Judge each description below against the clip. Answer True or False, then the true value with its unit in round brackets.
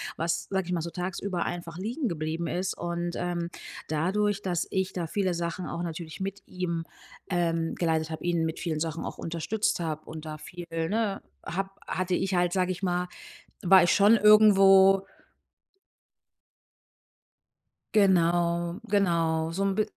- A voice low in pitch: False (175 Hz)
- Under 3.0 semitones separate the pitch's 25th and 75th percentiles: True (2.5 semitones)